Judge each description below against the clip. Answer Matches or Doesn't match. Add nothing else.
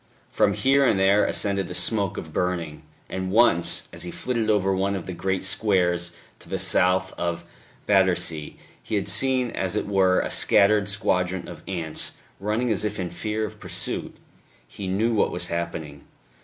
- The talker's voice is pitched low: Matches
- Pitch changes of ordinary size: Matches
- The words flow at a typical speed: Matches